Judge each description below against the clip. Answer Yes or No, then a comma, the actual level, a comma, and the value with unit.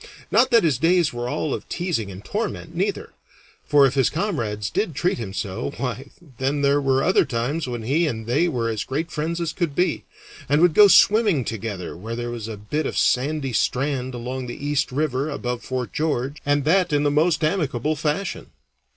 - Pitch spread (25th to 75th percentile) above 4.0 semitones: Yes, average, 5.1 semitones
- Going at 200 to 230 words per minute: Yes, fast, 205 wpm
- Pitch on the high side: No, medium, 140 Hz